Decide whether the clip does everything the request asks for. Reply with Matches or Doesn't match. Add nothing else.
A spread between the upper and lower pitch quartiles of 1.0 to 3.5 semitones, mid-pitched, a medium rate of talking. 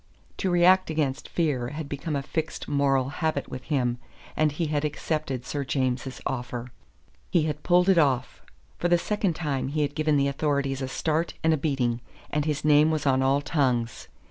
Matches